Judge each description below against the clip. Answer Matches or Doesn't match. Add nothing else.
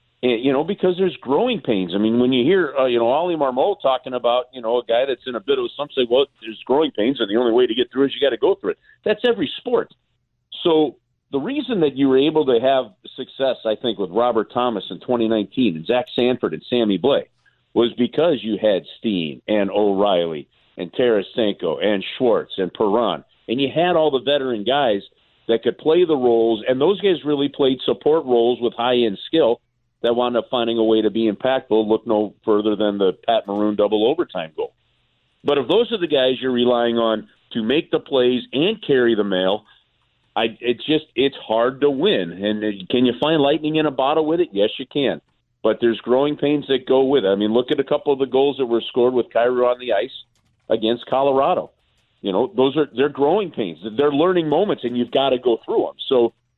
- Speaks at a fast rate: Matches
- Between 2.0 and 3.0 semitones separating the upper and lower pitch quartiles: Doesn't match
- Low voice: Matches